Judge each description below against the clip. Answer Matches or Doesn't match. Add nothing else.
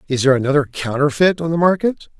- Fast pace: Doesn't match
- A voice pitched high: Doesn't match